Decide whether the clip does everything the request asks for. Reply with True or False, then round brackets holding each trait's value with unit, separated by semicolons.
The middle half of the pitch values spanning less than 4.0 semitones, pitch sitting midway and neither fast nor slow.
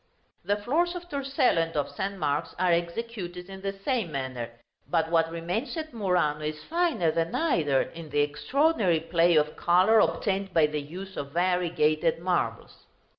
False (4.7 semitones; 175 Hz; 165 wpm)